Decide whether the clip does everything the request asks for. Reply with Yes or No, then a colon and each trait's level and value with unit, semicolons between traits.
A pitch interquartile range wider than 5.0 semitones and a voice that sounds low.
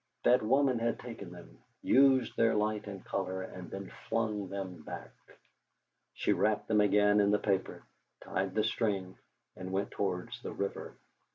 No: average, 2.7 semitones; low, 105 Hz